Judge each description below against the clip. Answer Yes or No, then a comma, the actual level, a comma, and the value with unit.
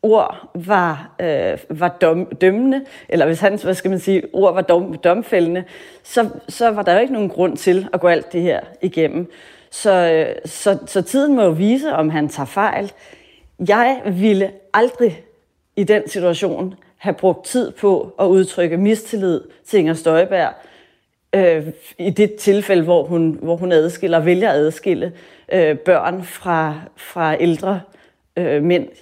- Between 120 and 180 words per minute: Yes, average, 155 wpm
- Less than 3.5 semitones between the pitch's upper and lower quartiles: Yes, average, 2.8 semitones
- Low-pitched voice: No, medium, 185 Hz